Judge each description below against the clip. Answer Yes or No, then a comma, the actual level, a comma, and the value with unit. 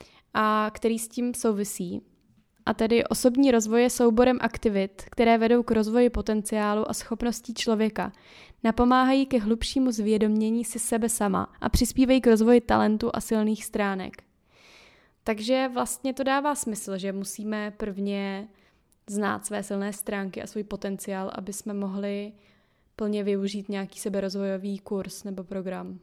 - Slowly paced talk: No, average, 140 wpm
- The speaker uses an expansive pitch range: No, average, 2.7 semitones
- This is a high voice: Yes, high, 215 Hz